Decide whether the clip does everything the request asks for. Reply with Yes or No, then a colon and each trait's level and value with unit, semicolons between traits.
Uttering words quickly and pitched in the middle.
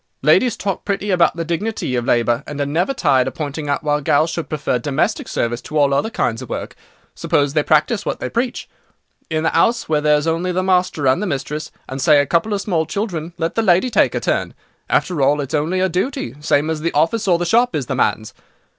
Yes: fast, 235 wpm; medium, 160 Hz